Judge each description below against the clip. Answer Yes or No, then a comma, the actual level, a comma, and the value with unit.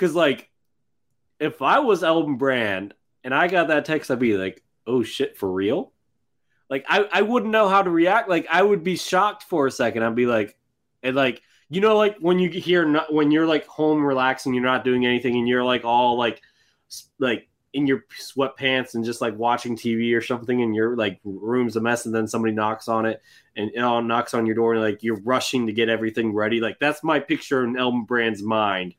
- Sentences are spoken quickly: Yes, fast, 225 wpm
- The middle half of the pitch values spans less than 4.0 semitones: No, average, 4.9 semitones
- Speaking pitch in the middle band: No, low, 125 Hz